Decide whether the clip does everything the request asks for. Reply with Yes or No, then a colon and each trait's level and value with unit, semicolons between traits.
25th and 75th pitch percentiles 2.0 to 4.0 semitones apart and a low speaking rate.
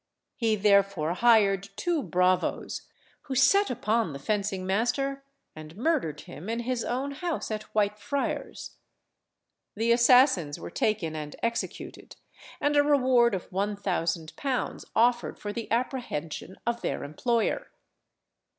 No: average, 5.2 semitones; slow, 130 wpm